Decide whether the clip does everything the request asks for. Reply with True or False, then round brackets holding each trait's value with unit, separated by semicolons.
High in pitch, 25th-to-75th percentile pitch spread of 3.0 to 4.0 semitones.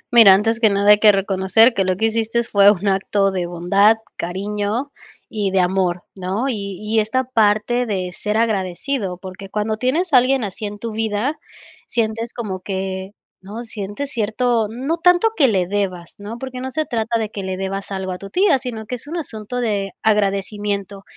True (210 Hz; 3.3 semitones)